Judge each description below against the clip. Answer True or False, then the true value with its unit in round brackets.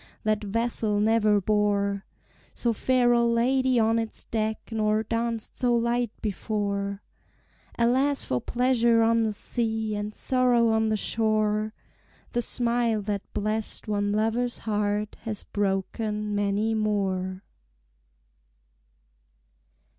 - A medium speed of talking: False (115 wpm)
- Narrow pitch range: True (2.0 semitones)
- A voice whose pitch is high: True (220 Hz)